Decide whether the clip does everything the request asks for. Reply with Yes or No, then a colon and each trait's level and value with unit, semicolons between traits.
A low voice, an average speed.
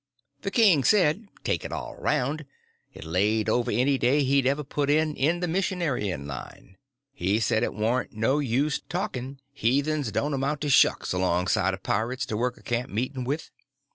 Yes: low, 130 Hz; average, 175 wpm